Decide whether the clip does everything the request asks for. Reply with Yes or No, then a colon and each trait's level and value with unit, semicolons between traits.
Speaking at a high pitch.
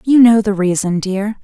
Yes: high, 205 Hz